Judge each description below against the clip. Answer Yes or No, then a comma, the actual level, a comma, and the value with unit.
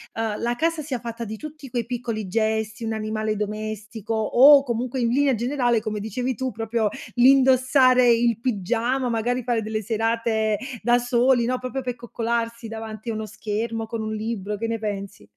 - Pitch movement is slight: Yes, narrow, 2.2 semitones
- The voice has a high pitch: Yes, high, 230 Hz